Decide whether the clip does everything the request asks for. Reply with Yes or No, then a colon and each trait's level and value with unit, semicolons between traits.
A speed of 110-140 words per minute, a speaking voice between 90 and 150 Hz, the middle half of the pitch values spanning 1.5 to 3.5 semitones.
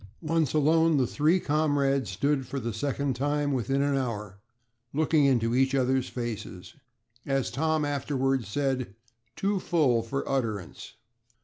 Yes: slow, 135 wpm; low, 135 Hz; average, 3.2 semitones